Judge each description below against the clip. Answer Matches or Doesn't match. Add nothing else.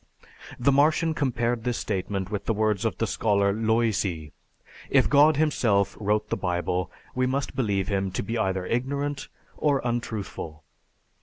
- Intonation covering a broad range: Doesn't match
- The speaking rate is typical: Matches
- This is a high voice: Doesn't match